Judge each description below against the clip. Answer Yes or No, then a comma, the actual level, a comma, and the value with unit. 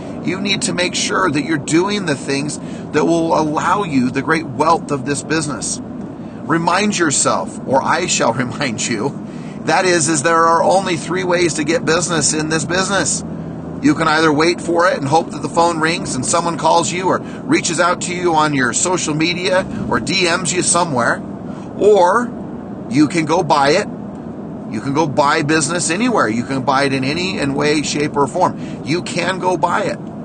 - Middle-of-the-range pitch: Yes, medium, 165 Hz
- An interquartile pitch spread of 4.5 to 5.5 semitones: No, average, 3.0 semitones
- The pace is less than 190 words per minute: No, average, 195 wpm